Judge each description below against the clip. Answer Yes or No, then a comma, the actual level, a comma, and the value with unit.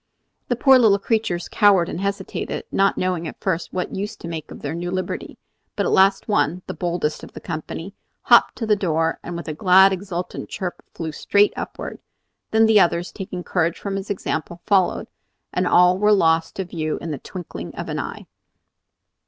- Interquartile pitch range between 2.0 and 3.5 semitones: Yes, average, 2.8 semitones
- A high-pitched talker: No, medium, 180 Hz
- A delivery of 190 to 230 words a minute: Yes, average, 195 wpm